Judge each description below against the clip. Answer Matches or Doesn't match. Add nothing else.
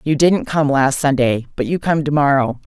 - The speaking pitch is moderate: Matches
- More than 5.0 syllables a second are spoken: Doesn't match